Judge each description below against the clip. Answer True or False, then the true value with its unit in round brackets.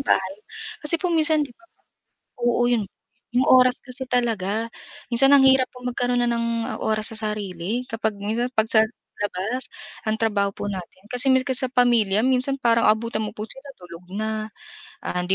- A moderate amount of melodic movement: True (3.1 semitones)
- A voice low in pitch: False (235 Hz)